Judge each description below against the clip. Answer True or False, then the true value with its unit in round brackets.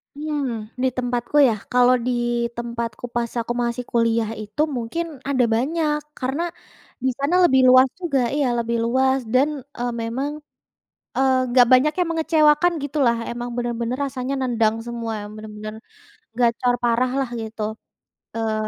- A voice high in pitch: True (245 Hz)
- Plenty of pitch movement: False (2.8 semitones)